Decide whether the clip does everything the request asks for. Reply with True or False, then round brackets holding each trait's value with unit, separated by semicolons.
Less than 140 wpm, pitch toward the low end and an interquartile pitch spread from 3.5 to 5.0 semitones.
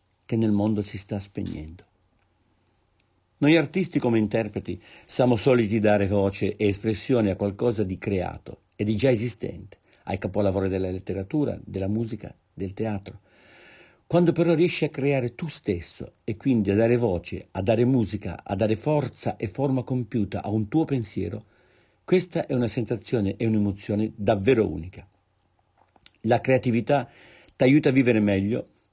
False (150 wpm; 110 Hz; 4.0 semitones)